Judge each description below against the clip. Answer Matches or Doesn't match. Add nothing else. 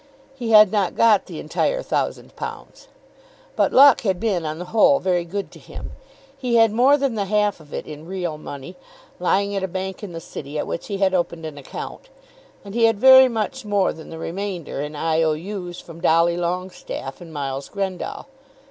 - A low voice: Doesn't match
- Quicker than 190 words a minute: Matches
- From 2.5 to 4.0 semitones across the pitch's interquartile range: Doesn't match